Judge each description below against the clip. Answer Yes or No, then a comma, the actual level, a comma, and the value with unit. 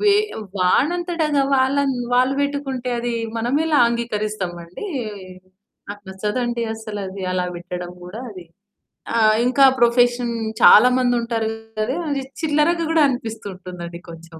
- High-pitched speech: Yes, high, 235 Hz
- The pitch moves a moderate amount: No, wide, 6.0 semitones